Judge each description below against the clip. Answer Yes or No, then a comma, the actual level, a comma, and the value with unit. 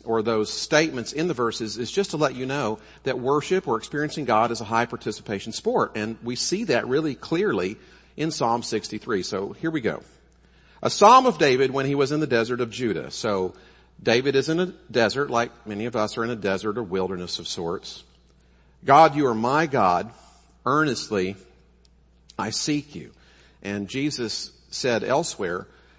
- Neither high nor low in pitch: No, low, 115 Hz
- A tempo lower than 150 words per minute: No, average, 180 wpm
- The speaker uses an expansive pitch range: Yes, wide, 6.7 semitones